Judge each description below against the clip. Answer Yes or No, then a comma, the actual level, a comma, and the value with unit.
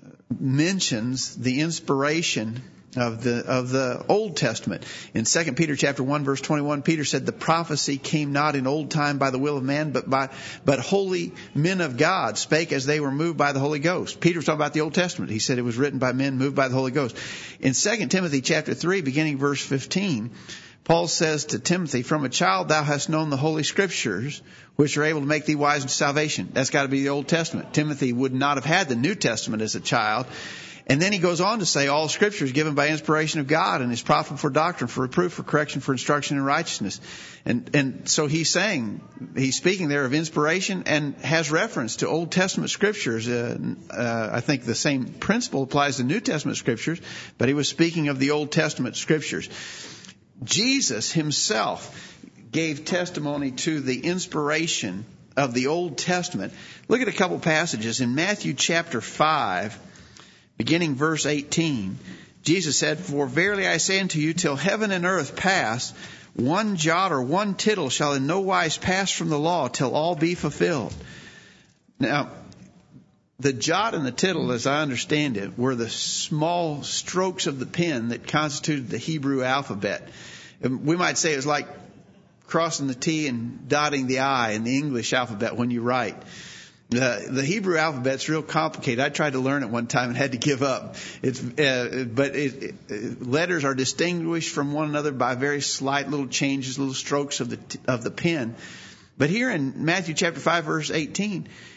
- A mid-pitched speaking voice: Yes, medium, 150 Hz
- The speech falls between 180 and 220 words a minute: Yes, average, 190 wpm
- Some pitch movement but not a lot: Yes, average, 3.5 semitones